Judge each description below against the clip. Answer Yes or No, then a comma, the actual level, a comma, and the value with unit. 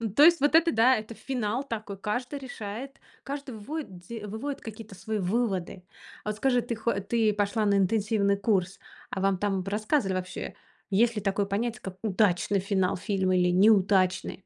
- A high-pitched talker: Yes, high, 210 Hz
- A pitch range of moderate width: Yes, average, 3.3 semitones